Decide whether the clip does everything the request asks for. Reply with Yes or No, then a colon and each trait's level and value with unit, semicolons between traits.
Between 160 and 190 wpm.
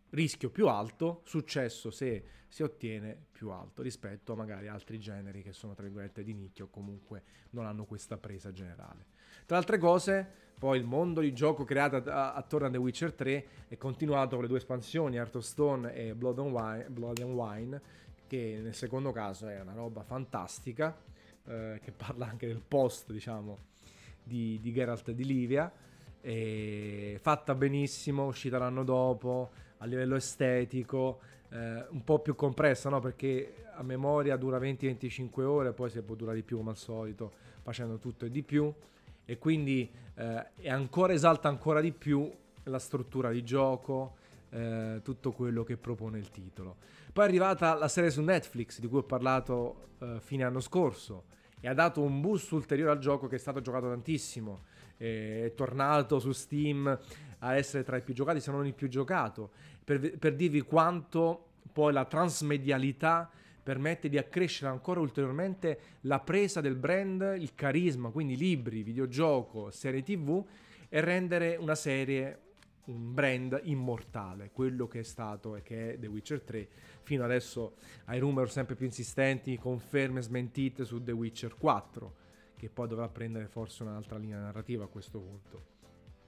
Yes: average, 165 wpm